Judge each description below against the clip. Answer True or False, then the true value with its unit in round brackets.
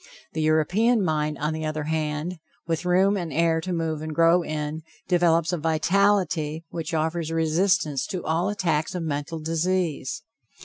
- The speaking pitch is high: False (165 Hz)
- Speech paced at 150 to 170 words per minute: True (160 wpm)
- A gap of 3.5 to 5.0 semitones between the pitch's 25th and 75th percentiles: False (2.4 semitones)